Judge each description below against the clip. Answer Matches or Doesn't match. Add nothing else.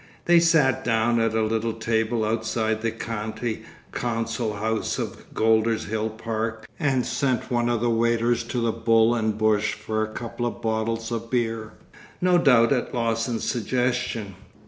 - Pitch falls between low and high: Doesn't match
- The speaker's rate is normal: Matches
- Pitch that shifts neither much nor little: Doesn't match